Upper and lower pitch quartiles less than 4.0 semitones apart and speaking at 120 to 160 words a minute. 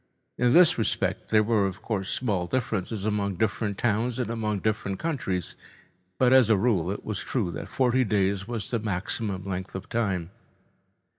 No: average, 3.3 semitones; average, 170 wpm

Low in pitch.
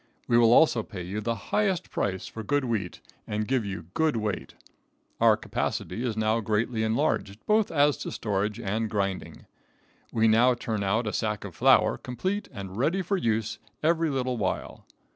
Yes: low, 115 Hz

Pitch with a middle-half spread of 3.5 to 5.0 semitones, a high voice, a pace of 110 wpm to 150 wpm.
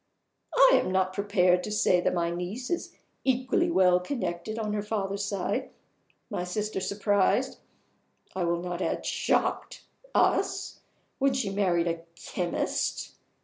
No: average, 3.0 semitones; high, 195 Hz; average, 140 wpm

